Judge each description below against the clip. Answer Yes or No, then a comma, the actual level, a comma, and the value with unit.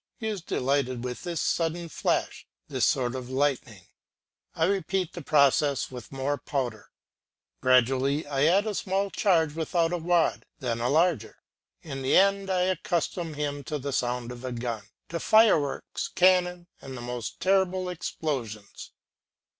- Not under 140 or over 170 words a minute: Yes, average, 155 wpm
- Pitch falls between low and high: Yes, medium, 145 Hz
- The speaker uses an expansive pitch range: Yes, wide, 5.7 semitones